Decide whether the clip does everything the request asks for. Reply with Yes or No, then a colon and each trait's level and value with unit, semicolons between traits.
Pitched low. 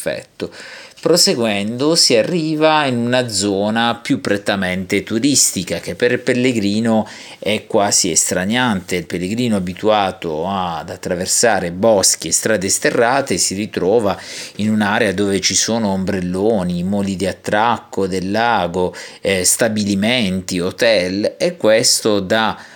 Yes: low, 105 Hz